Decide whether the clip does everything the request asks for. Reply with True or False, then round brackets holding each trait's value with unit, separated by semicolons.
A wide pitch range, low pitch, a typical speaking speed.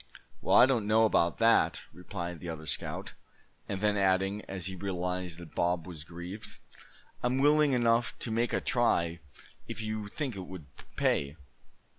False (4.7 semitones; 95 Hz; 165 wpm)